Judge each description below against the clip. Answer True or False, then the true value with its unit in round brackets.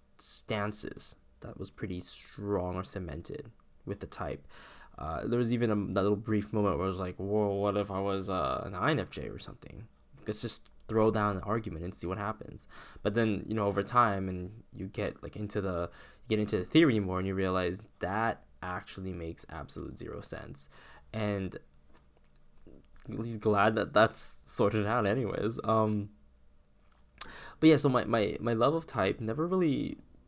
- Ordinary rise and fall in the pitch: True (3.2 semitones)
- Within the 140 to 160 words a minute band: False (180 wpm)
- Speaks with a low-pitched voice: True (100 Hz)